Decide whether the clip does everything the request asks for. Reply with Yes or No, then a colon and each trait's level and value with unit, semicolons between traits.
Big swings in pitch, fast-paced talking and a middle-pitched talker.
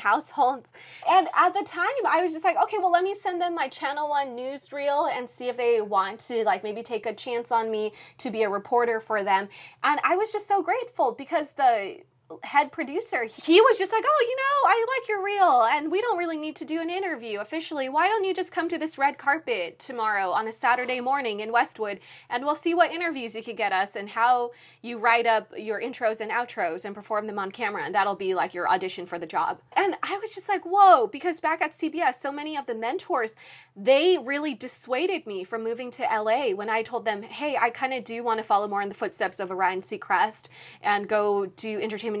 No: wide, 8.0 semitones; fast, 230 wpm; very high, 265 Hz